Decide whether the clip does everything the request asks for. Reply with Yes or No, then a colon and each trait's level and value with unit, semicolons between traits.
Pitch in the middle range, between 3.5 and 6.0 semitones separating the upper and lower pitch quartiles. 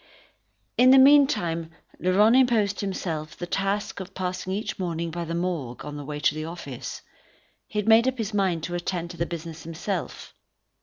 Yes: medium, 180 Hz; average, 4.0 semitones